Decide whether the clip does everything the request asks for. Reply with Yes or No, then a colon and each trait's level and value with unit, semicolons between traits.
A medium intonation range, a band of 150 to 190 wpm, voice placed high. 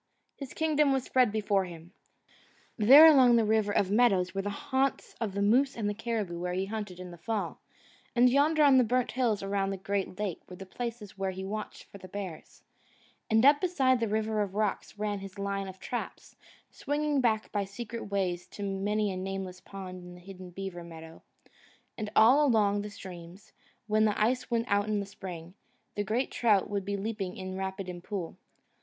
No: average, 3.3 semitones; average, 200 wpm; high, 205 Hz